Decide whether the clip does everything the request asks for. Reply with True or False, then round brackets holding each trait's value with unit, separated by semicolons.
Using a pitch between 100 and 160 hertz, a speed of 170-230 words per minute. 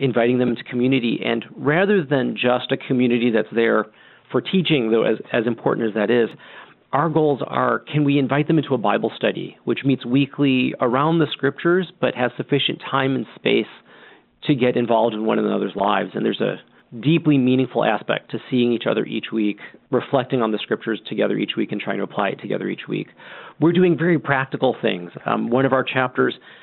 True (130 Hz; 200 wpm)